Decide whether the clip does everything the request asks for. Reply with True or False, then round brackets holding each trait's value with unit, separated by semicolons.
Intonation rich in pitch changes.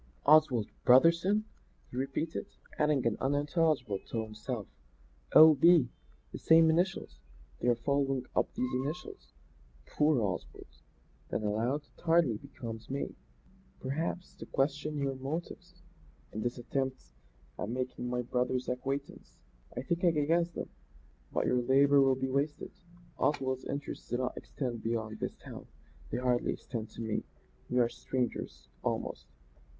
False (3.7 semitones)